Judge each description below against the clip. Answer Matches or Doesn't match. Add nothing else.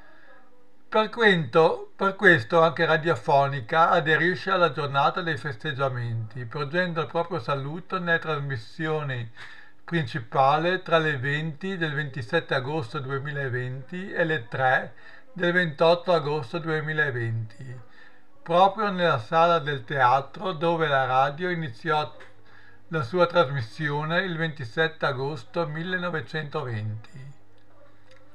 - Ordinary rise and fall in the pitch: Matches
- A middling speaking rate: Doesn't match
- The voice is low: Doesn't match